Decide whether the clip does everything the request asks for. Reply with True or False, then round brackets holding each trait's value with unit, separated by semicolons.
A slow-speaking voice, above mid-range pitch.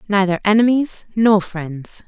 True (115 wpm; 200 Hz)